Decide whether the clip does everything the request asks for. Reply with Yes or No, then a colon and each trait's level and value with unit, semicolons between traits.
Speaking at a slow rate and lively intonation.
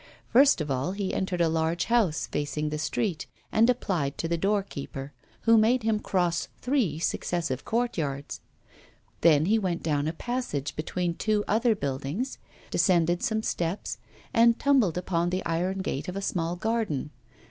No: average, 160 wpm; wide, 5.7 semitones